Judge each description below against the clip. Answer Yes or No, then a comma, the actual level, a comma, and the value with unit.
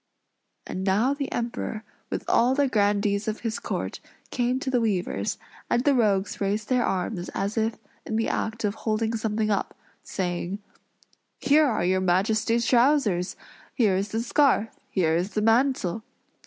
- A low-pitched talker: No, high, 220 Hz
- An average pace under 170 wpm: Yes, average, 160 wpm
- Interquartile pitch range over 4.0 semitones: No, average, 3.5 semitones